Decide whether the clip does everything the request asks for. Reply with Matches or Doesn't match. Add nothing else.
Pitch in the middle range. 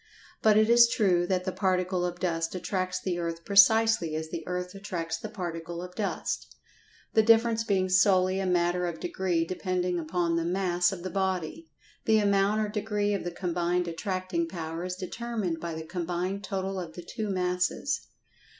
Matches